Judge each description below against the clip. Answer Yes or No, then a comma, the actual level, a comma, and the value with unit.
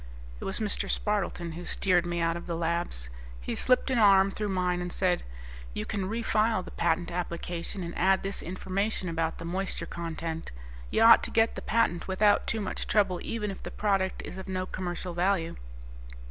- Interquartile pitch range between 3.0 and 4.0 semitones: No, narrow, 2.6 semitones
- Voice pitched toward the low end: No, medium, 185 Hz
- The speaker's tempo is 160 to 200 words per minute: Yes, average, 190 wpm